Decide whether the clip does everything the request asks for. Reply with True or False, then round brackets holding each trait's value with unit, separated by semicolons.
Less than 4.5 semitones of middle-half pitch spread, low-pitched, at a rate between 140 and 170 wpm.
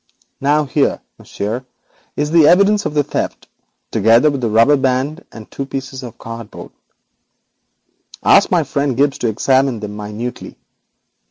True (4.1 semitones; 130 Hz; 145 wpm)